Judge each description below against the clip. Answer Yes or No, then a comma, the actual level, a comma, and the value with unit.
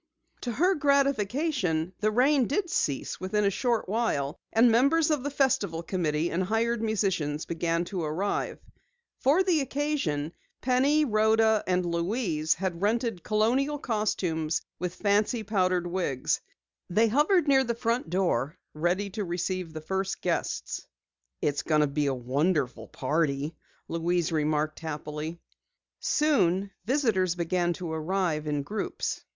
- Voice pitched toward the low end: No, high, 190 Hz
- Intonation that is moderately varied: No, wide, 6.5 semitones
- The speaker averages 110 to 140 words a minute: Yes, slow, 135 wpm